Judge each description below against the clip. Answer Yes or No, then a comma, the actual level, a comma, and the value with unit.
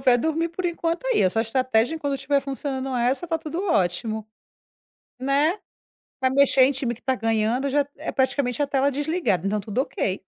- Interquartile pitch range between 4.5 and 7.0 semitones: No, average, 3.7 semitones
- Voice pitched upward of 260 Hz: Yes, very high, 270 Hz